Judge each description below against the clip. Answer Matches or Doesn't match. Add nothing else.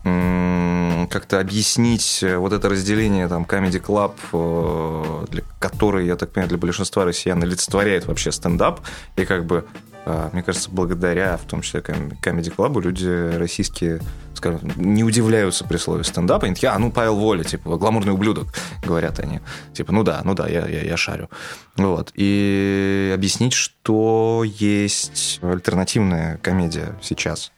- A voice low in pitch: Matches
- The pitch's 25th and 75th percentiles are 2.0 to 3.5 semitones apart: Matches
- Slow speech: Doesn't match